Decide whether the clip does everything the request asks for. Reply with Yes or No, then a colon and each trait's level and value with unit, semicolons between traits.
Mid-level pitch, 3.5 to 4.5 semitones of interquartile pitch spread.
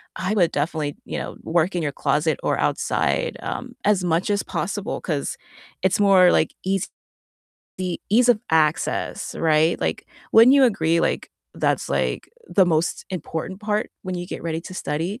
Yes: medium, 175 Hz; average, 3.8 semitones